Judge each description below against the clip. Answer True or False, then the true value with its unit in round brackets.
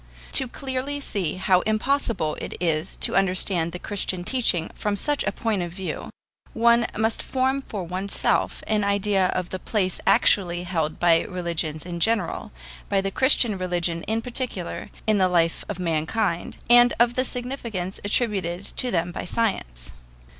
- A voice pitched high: True (195 Hz)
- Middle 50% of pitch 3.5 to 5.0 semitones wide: True (4.7 semitones)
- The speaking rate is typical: True (160 wpm)